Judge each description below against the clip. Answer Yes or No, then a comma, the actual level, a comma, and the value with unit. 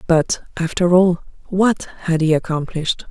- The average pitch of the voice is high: No, medium, 170 Hz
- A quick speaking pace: No, slow, 135 wpm